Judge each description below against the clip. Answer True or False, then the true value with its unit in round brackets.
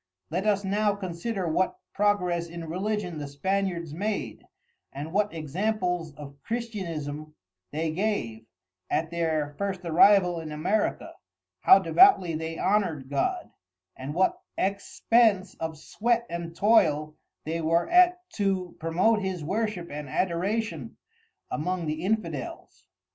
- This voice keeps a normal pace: False (125 wpm)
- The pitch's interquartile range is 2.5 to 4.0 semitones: False (4.5 semitones)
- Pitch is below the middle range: False (180 Hz)